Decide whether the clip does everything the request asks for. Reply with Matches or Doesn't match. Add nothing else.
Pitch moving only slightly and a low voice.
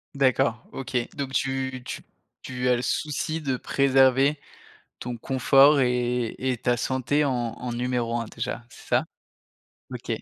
Matches